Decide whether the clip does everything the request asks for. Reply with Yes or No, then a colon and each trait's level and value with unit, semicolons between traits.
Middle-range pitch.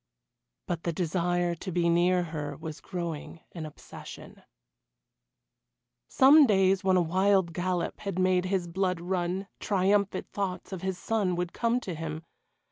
Yes: medium, 180 Hz